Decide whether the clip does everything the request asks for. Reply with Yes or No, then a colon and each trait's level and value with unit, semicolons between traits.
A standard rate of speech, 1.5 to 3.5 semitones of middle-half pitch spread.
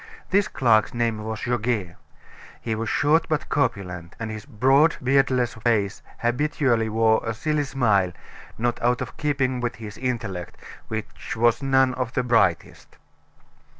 Yes: average, 145 wpm; average, 3.2 semitones